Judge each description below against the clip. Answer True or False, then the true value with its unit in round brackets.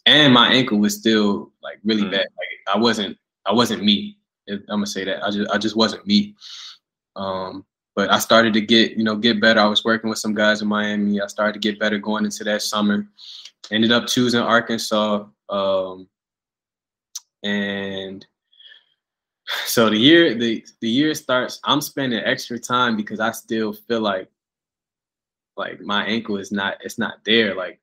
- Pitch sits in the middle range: False (110 Hz)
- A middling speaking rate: True (175 wpm)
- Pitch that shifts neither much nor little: False (2.0 semitones)